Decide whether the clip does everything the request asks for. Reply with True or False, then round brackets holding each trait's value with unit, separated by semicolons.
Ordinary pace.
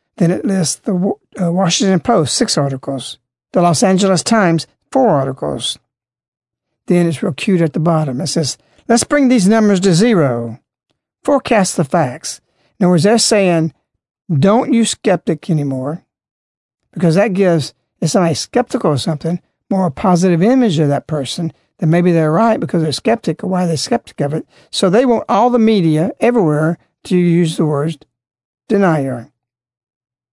True (160 wpm)